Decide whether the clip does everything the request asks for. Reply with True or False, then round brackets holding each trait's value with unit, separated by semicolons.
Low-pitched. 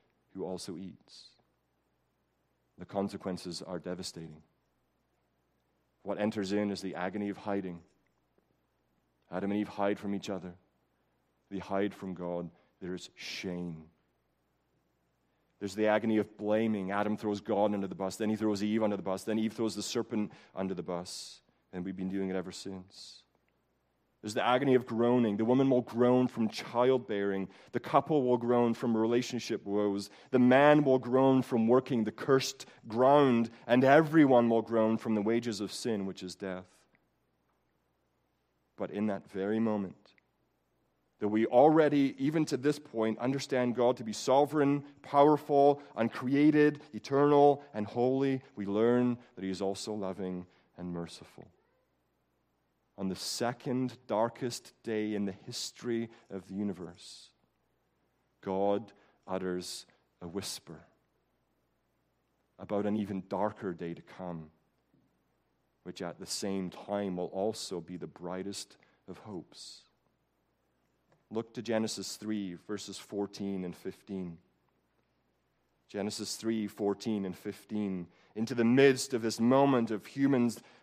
True (100 Hz)